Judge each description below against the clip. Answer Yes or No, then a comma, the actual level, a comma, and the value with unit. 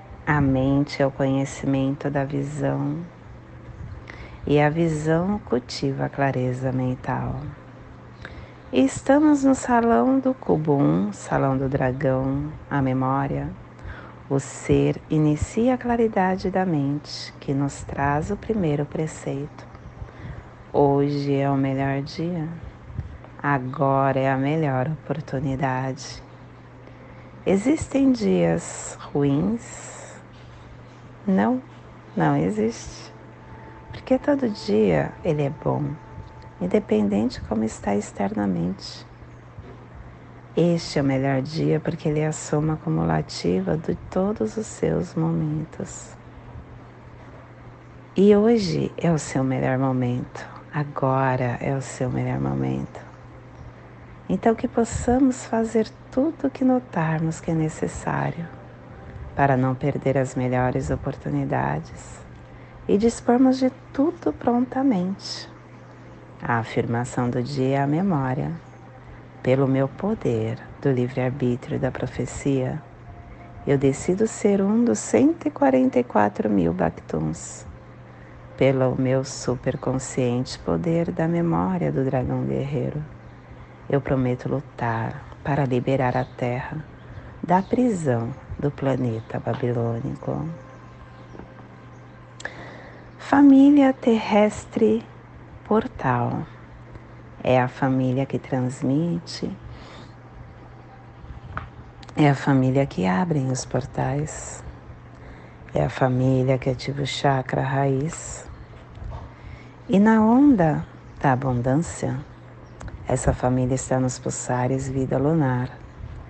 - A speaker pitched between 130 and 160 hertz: Yes, low, 135 Hz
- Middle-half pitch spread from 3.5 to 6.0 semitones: Yes, average, 4.5 semitones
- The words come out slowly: Yes, slow, 100 wpm